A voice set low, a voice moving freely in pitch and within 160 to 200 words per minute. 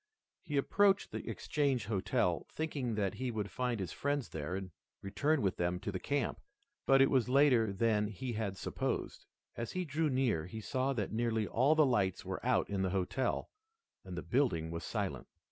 Yes: low, 115 Hz; wide, 5.9 semitones; average, 190 wpm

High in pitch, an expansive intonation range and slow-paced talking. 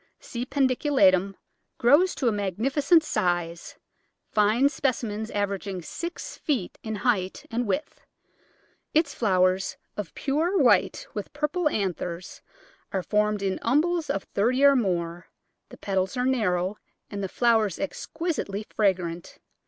Yes: high, 215 Hz; wide, 6.5 semitones; slow, 125 wpm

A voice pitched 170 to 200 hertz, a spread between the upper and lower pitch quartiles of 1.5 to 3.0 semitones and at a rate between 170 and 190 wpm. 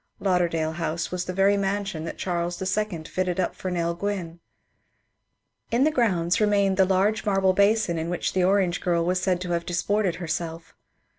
Yes: medium, 185 Hz; narrow, 2.6 semitones; average, 175 wpm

